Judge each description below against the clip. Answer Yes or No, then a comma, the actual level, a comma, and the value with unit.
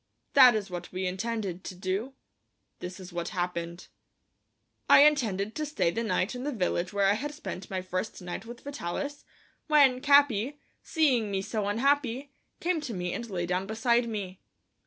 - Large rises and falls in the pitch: Yes, wide, 6.4 semitones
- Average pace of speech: Yes, average, 175 wpm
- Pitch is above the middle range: Yes, high, 215 Hz